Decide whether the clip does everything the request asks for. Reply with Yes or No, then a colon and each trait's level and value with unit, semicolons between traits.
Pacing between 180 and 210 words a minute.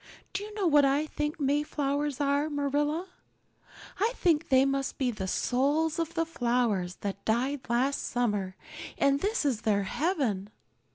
No: average, 155 wpm